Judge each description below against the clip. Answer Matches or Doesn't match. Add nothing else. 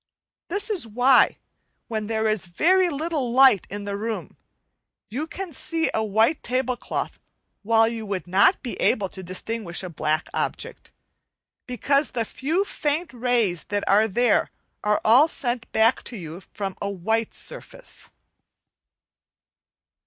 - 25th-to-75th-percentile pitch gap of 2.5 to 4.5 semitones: Doesn't match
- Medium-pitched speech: Doesn't match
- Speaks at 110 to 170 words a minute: Matches